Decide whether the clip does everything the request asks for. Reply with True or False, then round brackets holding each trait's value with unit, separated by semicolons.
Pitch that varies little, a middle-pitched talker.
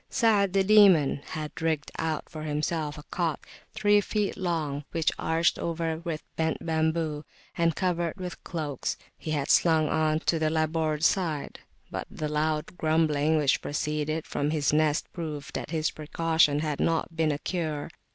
True (1.8 semitones; 160 Hz)